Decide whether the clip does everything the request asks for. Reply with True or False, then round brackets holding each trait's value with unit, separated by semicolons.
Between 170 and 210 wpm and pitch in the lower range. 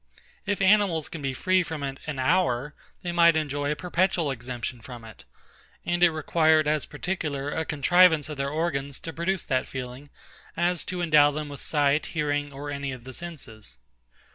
False (180 wpm; 150 Hz)